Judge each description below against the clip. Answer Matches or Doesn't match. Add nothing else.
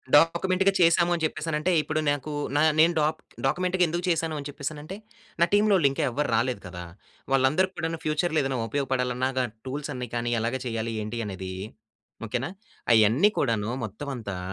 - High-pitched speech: Doesn't match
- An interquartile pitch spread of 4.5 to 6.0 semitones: Matches